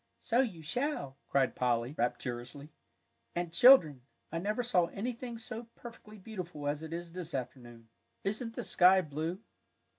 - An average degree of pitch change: No, wide, 7.9 semitones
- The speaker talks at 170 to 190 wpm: No, average, 145 wpm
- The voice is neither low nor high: Yes, medium, 170 Hz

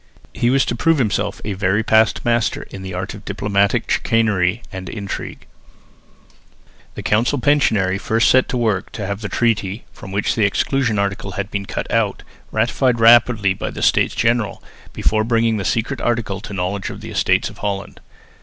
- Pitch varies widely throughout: No, average, 2.9 semitones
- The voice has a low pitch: Yes, low, 110 Hz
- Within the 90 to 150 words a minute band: No, average, 180 wpm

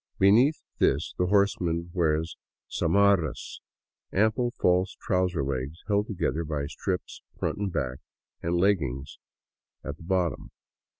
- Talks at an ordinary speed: No, slow, 125 wpm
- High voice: No, very low, 90 Hz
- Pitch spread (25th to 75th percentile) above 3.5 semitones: Yes, average, 4.3 semitones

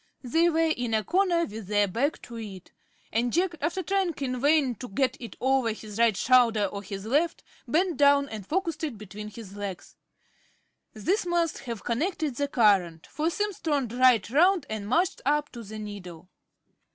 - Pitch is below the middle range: No, very high, 250 Hz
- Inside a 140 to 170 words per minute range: No, average, 180 wpm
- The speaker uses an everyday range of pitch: No, wide, 7.1 semitones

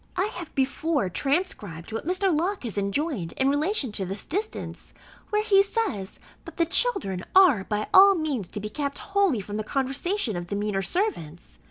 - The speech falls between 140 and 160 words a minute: No, average, 180 wpm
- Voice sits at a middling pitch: No, very high, 280 Hz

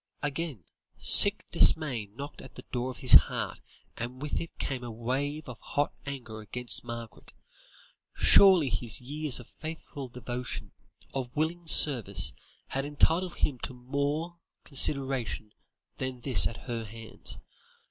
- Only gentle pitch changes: No, average, 3.8 semitones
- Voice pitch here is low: Yes, low, 130 Hz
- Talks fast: No, slow, 135 wpm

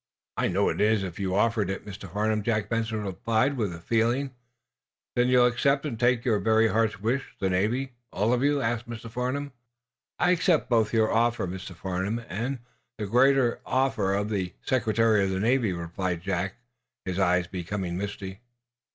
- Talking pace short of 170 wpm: No, average, 175 wpm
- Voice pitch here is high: No, low, 110 Hz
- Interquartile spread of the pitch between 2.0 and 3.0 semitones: No, average, 4.0 semitones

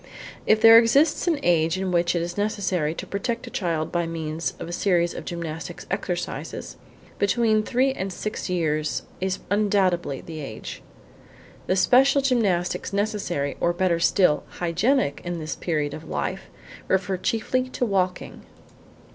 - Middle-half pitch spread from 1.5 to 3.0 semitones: No, average, 4.2 semitones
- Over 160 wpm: No, average, 150 wpm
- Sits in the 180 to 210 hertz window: Yes, medium, 185 Hz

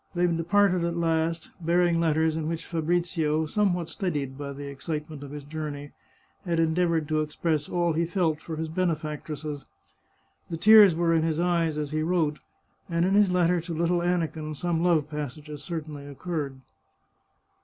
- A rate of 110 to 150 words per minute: No, average, 165 wpm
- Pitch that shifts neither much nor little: No, narrow, 2.2 semitones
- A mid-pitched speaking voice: Yes, medium, 160 Hz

